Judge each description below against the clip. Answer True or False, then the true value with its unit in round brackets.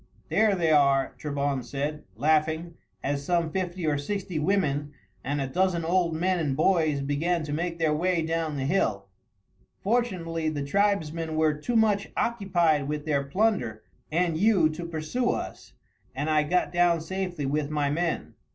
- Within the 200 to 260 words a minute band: False (160 wpm)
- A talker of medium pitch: True (160 Hz)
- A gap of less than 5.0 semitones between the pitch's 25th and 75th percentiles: True (3.5 semitones)